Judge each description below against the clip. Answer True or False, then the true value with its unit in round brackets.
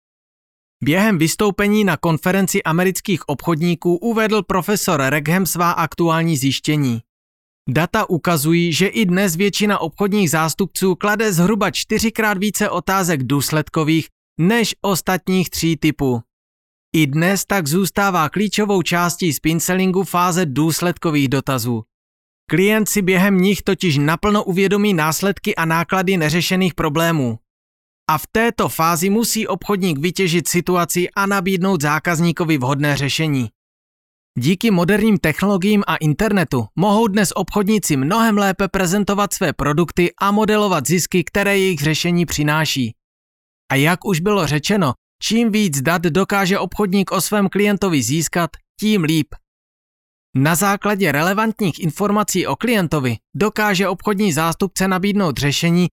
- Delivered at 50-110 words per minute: False (120 wpm)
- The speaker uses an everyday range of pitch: True (4.3 semitones)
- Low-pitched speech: False (180 Hz)